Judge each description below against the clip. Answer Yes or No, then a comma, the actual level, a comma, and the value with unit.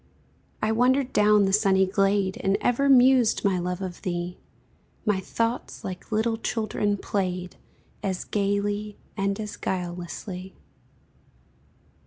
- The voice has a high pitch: Yes, high, 200 Hz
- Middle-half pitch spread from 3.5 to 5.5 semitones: No, narrow, 2.6 semitones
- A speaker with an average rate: No, slow, 120 wpm